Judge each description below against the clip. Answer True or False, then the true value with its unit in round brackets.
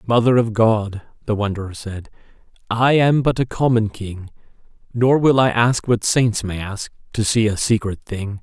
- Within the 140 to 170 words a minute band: False (180 wpm)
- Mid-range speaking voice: False (110 Hz)